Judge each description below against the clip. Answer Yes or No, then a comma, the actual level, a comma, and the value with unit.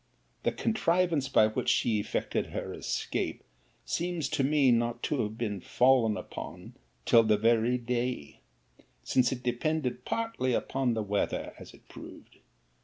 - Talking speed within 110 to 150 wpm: Yes, average, 145 wpm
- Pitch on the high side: No, low, 125 Hz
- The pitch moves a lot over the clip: No, average, 3.8 semitones